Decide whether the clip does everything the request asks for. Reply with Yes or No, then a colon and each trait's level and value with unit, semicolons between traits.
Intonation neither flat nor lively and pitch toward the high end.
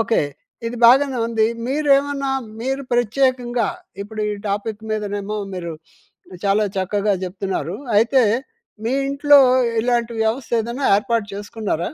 Yes: average, 4.1 semitones; high, 230 Hz